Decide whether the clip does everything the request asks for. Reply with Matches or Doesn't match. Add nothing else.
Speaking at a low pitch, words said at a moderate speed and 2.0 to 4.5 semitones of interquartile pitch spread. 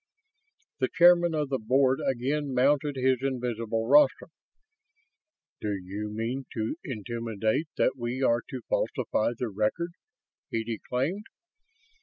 Doesn't match